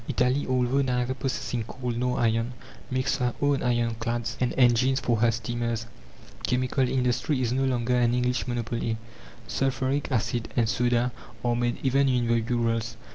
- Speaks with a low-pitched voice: Yes, low, 125 Hz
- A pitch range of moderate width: No, narrow, 1.6 semitones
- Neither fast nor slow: Yes, average, 160 wpm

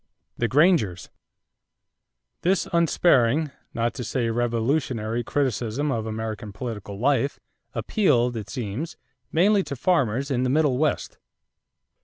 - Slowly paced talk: Yes, slow, 115 wpm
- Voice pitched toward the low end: Yes, low, 125 Hz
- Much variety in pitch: No, average, 4.6 semitones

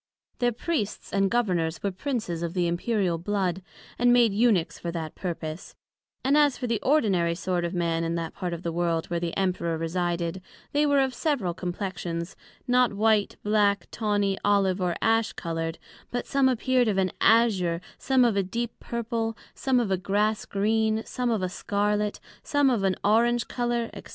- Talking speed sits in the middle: Yes, average, 180 wpm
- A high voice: Yes, high, 200 Hz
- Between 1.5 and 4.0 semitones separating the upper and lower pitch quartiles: No, average, 5.2 semitones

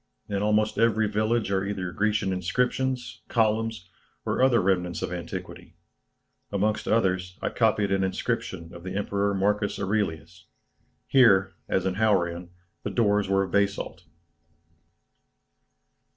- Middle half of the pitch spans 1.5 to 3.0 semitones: Yes, average, 2.7 semitones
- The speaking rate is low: Yes, slow, 125 wpm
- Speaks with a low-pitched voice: Yes, low, 100 Hz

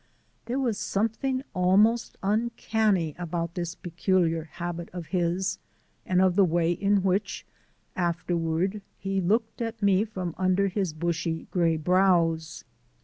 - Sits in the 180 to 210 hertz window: Yes, medium, 185 Hz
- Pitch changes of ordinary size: Yes, average, 3.0 semitones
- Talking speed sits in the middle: No, slow, 130 wpm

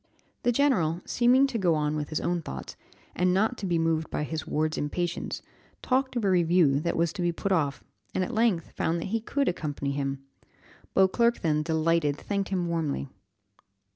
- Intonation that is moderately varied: Yes, average, 4.4 semitones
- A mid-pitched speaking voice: Yes, medium, 170 Hz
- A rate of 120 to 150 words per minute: No, average, 190 wpm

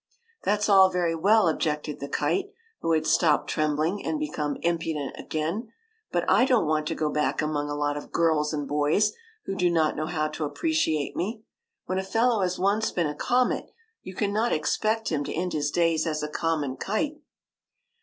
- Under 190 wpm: No, average, 195 wpm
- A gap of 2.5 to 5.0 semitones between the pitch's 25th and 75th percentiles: No, wide, 5.4 semitones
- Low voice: No, medium, 165 Hz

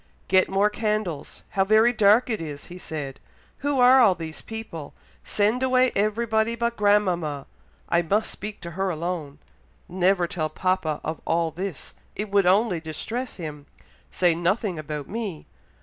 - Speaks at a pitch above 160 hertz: Yes, high, 190 Hz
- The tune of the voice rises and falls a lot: No, average, 4.9 semitones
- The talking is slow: No, average, 155 wpm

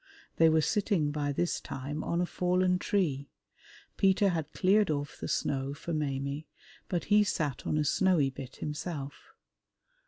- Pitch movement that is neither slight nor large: Yes, average, 4.2 semitones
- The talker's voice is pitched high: No, medium, 155 Hz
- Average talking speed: Yes, average, 155 wpm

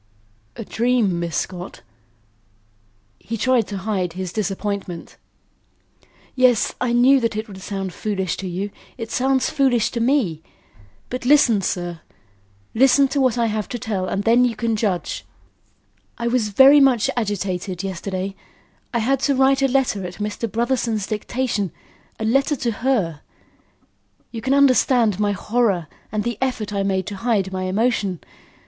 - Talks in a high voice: Yes, high, 220 Hz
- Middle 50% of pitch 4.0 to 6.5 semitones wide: Yes, average, 4.4 semitones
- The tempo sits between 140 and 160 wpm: Yes, average, 155 wpm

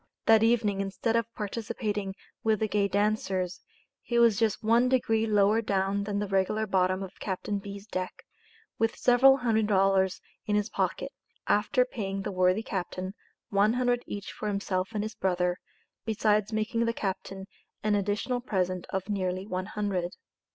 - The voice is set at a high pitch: Yes, high, 205 Hz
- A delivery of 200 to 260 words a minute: No, average, 160 wpm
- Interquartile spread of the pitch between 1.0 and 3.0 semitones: Yes, narrow, 2.5 semitones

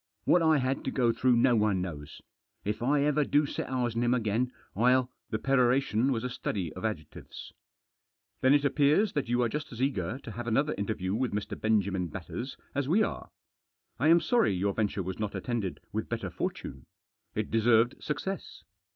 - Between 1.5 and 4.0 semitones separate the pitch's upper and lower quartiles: No, average, 4.6 semitones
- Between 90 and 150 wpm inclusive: No, average, 195 wpm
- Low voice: Yes, low, 120 Hz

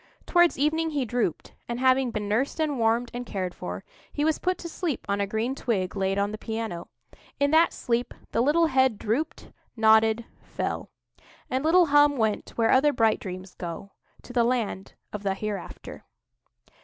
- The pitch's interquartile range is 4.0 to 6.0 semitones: Yes, wide, 5.4 semitones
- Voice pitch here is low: No, high, 235 Hz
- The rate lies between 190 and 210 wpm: No, average, 165 wpm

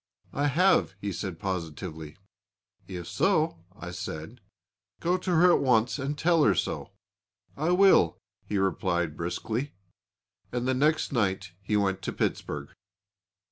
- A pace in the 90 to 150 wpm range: Yes, average, 140 wpm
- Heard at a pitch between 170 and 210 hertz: No, low, 105 Hz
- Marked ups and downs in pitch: Yes, wide, 8.9 semitones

